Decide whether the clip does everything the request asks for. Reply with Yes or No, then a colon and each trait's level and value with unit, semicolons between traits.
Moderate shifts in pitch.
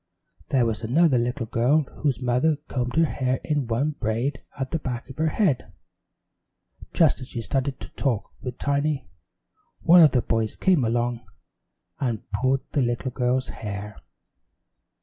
Yes: average, 3.3 semitones